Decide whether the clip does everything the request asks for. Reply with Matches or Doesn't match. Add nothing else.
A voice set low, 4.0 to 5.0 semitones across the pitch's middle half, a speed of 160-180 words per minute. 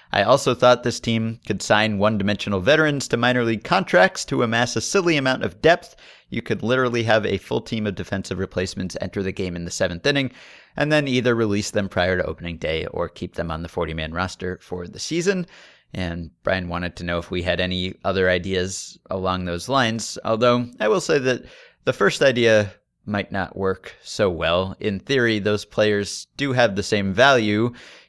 Doesn't match